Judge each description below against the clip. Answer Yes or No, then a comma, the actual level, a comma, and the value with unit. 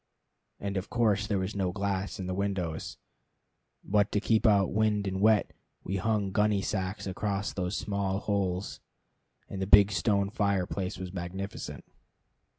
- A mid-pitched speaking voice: No, low, 100 Hz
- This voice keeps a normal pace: Yes, average, 155 wpm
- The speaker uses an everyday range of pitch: No, narrow, 1.6 semitones